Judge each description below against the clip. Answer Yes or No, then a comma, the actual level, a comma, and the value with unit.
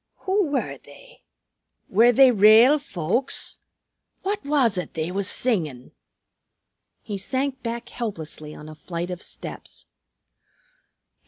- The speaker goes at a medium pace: No, slow, 115 wpm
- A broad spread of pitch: Yes, wide, 7.3 semitones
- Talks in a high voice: Yes, high, 225 Hz